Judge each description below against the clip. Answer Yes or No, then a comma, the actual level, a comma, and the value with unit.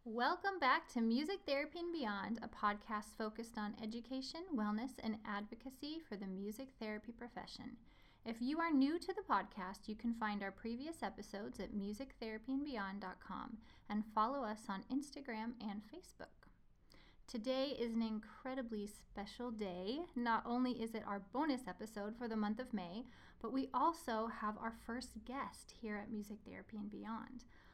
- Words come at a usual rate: Yes, average, 160 wpm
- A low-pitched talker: No, high, 230 Hz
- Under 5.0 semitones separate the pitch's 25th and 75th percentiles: Yes, average, 3.7 semitones